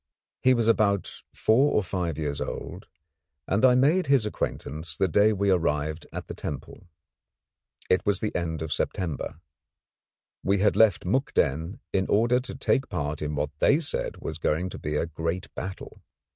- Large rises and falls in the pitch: Yes, wide, 5.9 semitones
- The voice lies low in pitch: Yes, very low, 95 Hz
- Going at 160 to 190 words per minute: Yes, average, 170 wpm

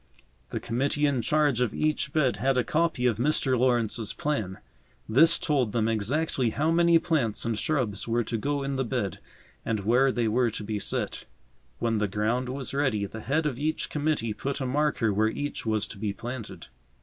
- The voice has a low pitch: Yes, low, 125 Hz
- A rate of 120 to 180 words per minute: No, average, 195 wpm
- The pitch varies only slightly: No, average, 4.6 semitones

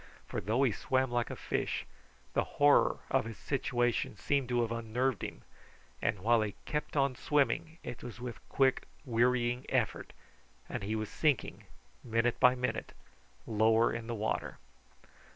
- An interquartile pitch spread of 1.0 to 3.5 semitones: Yes, narrow, 2.6 semitones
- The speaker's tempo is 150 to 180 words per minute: Yes, average, 155 wpm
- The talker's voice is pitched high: No, low, 120 Hz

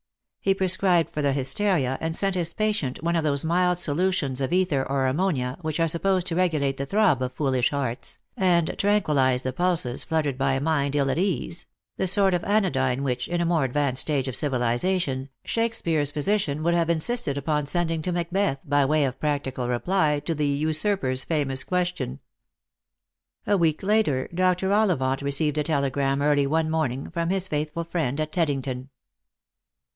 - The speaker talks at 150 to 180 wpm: Yes, average, 175 wpm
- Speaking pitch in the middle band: Yes, medium, 155 Hz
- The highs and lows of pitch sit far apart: No, average, 4.6 semitones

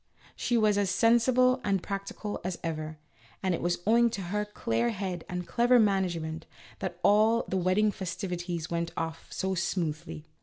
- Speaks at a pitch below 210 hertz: Yes, high, 190 Hz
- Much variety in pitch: No, average, 3.9 semitones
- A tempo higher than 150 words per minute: Yes, average, 165 wpm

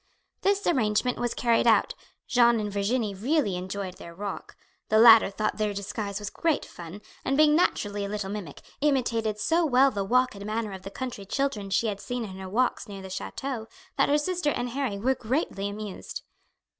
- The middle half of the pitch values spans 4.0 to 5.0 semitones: Yes, average, 4.3 semitones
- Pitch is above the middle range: Yes, high, 215 Hz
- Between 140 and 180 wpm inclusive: No, average, 195 wpm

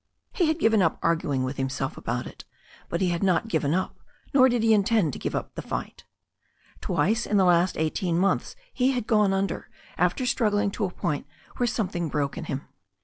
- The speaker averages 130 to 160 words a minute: No, fast, 205 wpm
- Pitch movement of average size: No, wide, 5.7 semitones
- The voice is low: No, high, 190 Hz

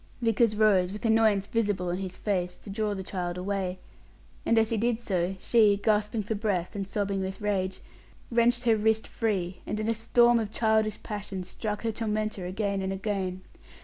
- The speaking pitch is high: Yes, high, 210 Hz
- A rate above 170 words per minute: Yes, average, 185 wpm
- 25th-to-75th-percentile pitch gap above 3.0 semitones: No, narrow, 2.6 semitones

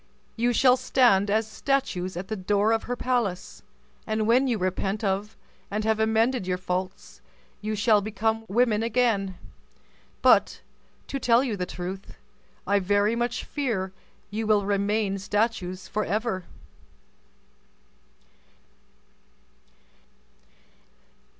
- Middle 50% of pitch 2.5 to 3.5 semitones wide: Yes, average, 3.1 semitones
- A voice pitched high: Yes, high, 215 Hz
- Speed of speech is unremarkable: No, slow, 115 wpm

